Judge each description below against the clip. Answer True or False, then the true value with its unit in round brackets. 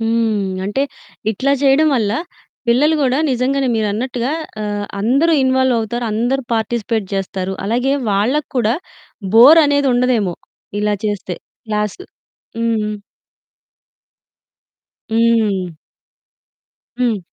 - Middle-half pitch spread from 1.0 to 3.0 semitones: False (3.7 semitones)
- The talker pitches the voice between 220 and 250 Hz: True (230 Hz)